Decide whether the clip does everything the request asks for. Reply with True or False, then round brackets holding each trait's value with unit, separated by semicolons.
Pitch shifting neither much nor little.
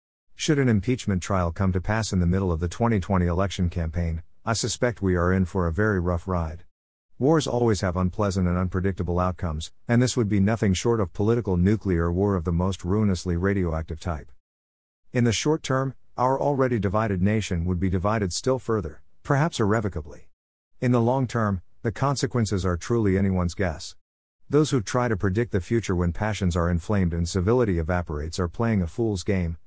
True (4.7 semitones)